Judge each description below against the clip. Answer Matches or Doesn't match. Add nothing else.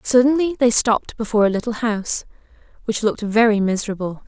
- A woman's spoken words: Matches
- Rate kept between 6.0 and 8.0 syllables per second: Matches